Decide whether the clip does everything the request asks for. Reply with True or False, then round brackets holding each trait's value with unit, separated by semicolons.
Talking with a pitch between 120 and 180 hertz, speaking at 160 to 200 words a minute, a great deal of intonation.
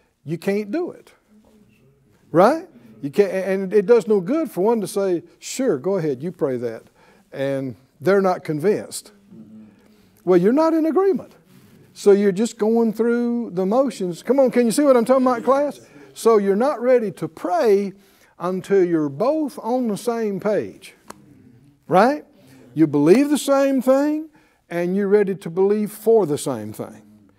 False (205 Hz; 165 wpm; 5.7 semitones)